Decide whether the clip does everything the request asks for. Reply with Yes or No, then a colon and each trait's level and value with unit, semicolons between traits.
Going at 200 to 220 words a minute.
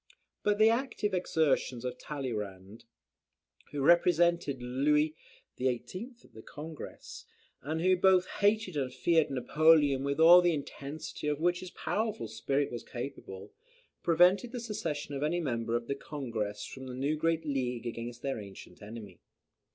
No: average, 150 wpm